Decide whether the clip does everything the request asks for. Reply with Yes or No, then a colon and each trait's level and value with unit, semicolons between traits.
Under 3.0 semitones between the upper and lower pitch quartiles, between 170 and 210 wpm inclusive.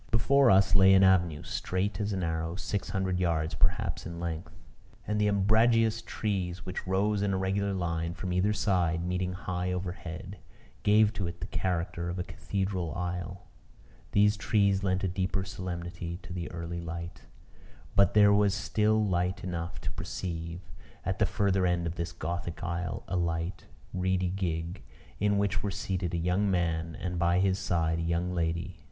Yes: narrow, 2.4 semitones; average, 175 wpm